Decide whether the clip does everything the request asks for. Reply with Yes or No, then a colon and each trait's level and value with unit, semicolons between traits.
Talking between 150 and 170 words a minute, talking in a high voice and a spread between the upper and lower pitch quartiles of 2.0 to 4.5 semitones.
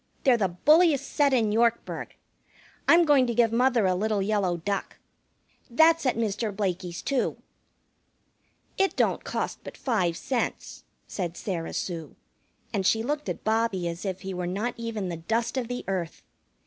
No: average, 160 wpm; high, 220 Hz; average, 4.9 semitones